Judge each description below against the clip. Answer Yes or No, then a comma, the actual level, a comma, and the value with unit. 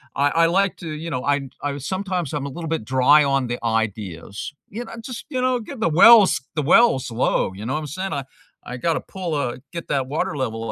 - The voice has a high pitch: No, medium, 150 Hz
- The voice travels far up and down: Yes, wide, 6.4 semitones